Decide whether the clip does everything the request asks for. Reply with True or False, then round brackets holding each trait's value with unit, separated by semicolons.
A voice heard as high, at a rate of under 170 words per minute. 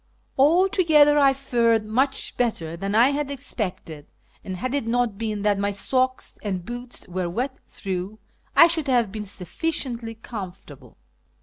True (230 Hz; 145 wpm)